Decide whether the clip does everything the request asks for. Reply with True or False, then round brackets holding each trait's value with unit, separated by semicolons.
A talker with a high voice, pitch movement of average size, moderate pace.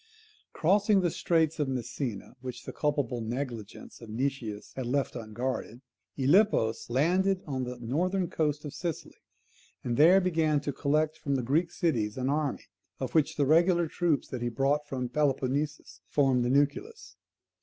False (140 Hz; 4.2 semitones; 155 wpm)